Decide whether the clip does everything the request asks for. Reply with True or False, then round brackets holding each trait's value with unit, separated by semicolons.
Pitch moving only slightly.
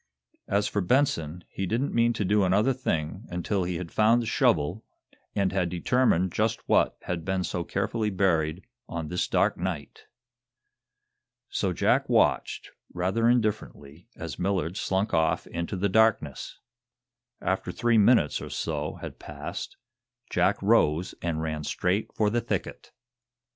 False (4.4 semitones)